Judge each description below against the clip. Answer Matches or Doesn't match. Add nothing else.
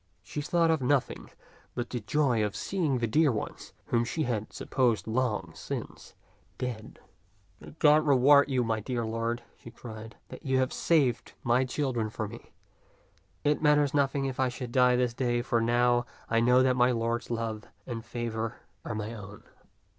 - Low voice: Matches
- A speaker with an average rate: Matches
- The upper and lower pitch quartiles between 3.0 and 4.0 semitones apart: Doesn't match